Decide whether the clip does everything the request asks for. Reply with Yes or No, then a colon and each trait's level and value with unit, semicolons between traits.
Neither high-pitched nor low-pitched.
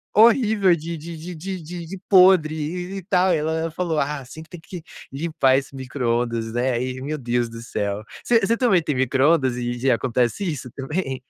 Yes: medium, 150 Hz